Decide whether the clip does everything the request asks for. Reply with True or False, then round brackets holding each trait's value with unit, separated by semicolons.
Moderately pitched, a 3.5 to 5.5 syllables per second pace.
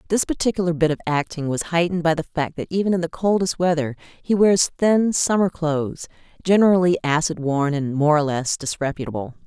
False (165 Hz; 5.7 syllables/s)